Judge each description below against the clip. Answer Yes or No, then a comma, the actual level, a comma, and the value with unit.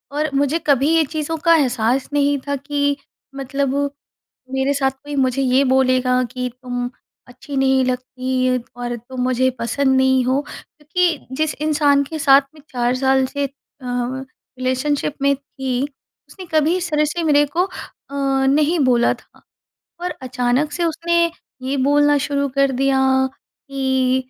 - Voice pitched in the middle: No, very high, 275 Hz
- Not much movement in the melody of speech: Yes, narrow, 2.2 semitones